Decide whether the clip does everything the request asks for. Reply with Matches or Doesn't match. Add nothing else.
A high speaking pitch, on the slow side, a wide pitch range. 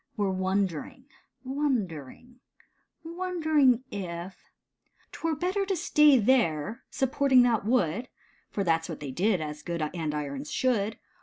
Matches